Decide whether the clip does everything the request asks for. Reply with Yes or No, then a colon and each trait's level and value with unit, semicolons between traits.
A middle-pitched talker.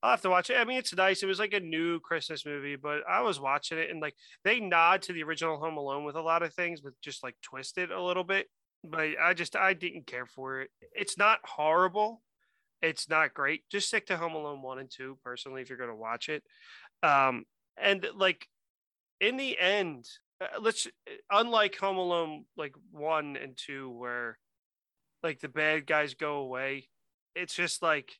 Yes: medium, 160 Hz